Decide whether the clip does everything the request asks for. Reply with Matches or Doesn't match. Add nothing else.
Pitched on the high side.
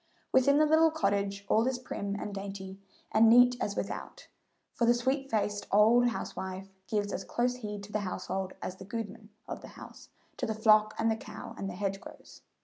Matches